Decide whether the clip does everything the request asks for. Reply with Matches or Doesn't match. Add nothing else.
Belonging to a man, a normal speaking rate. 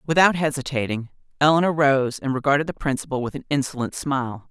Doesn't match